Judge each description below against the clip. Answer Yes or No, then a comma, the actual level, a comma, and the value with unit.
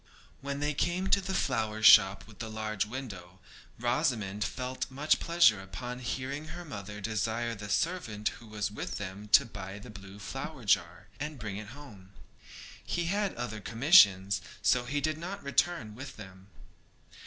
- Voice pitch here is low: Yes, low, 115 Hz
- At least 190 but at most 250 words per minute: No, average, 155 wpm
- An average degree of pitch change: No, wide, 5.8 semitones